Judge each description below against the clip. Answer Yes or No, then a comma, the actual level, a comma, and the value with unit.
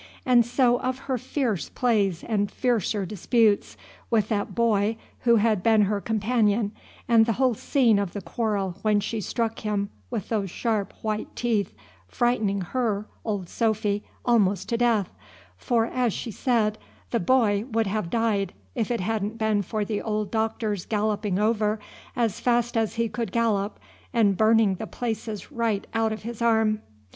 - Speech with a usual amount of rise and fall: No, narrow, 2.3 semitones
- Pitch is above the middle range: Yes, high, 220 Hz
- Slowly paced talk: No, average, 165 wpm